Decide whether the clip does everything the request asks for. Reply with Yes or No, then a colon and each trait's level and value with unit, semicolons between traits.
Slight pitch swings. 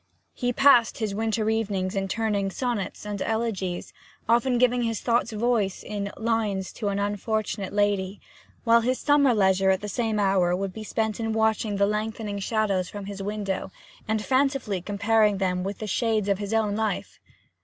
Yes: narrow, 2.3 semitones